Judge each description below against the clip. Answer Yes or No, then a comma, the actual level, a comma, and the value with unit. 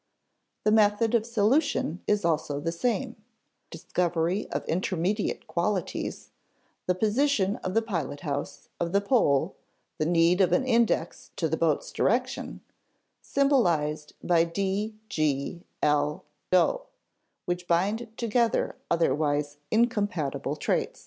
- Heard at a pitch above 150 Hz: Yes, medium, 185 Hz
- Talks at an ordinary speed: No, slow, 120 wpm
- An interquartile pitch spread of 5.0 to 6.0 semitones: Yes, average, 5.3 semitones